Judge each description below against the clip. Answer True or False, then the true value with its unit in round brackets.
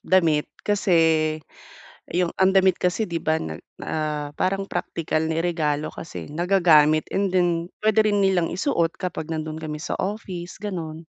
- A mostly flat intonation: False (3.2 semitones)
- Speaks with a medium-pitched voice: True (170 Hz)